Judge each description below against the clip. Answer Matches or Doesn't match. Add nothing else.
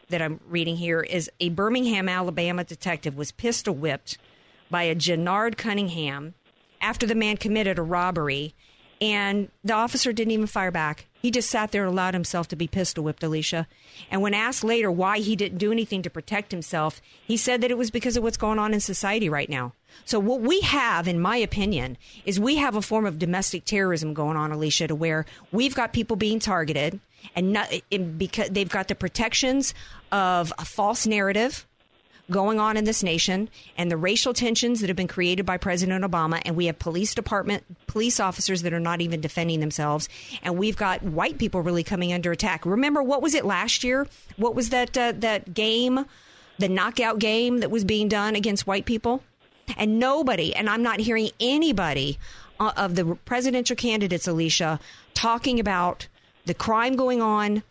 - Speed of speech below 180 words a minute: Doesn't match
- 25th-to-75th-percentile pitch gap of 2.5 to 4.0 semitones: Doesn't match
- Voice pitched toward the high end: Matches